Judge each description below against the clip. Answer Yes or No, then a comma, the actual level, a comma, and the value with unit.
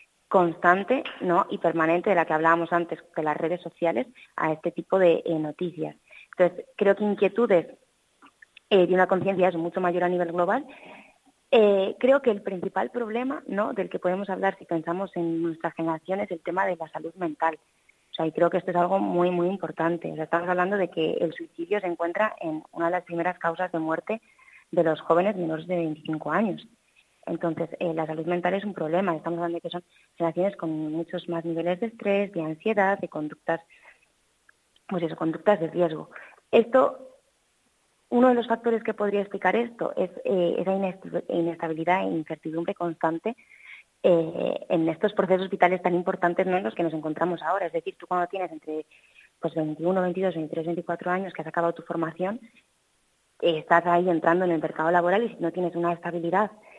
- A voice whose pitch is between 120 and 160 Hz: No, medium, 175 Hz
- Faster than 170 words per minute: Yes, fast, 190 wpm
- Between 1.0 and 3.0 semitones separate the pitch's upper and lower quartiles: Yes, average, 2.7 semitones